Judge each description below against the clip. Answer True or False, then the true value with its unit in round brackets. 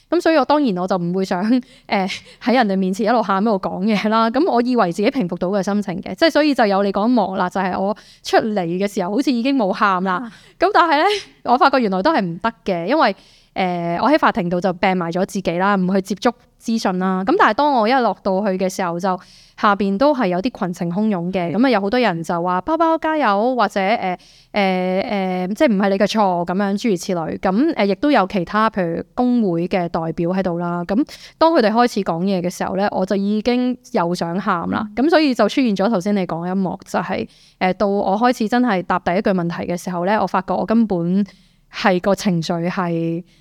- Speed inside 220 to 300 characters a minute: False (330 characters per minute)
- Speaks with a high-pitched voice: True (200 Hz)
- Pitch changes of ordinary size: True (4.2 semitones)